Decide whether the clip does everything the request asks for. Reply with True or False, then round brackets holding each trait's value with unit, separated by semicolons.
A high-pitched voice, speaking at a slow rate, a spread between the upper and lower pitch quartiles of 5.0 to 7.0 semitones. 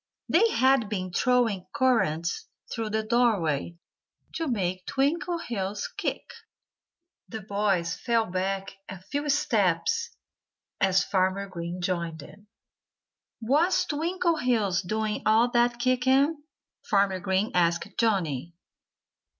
True (210 Hz; 105 wpm; 5.5 semitones)